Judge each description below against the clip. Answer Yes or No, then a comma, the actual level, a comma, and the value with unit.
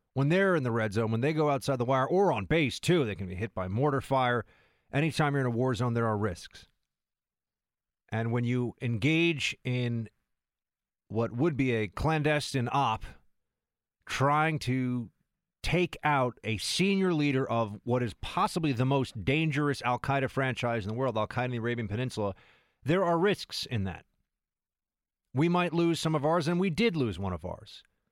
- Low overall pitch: Yes, low, 130 Hz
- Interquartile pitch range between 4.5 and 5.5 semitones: Yes, average, 4.9 semitones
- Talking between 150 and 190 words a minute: Yes, average, 185 wpm